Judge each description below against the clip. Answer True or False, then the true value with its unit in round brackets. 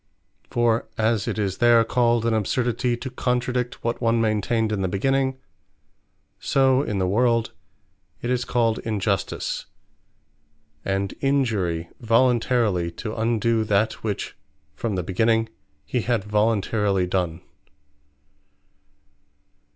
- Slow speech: True (115 wpm)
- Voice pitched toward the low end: True (115 Hz)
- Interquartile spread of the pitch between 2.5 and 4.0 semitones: True (3.0 semitones)